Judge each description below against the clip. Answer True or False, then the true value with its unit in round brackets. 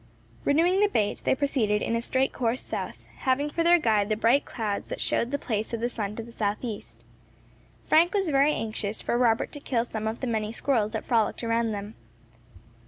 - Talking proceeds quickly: True (210 wpm)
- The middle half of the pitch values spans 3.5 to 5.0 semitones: True (4.2 semitones)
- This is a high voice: True (230 Hz)